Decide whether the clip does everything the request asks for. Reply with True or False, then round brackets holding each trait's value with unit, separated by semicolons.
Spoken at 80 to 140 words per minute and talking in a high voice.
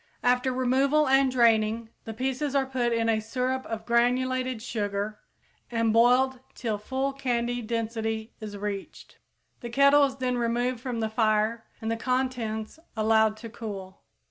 False (150 wpm; 235 Hz)